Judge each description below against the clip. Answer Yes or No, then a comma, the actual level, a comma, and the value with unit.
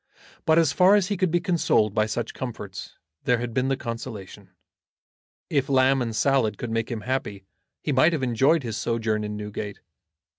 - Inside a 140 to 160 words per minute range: No, average, 185 wpm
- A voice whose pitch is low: Yes, low, 125 Hz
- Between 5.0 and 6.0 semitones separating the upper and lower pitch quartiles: No, average, 4.3 semitones